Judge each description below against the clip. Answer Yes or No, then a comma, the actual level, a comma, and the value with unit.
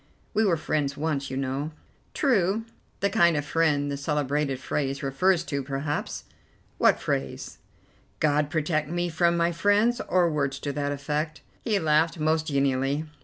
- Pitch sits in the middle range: Yes, medium, 150 Hz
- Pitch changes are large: No, average, 3.3 semitones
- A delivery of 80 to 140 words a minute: No, average, 155 wpm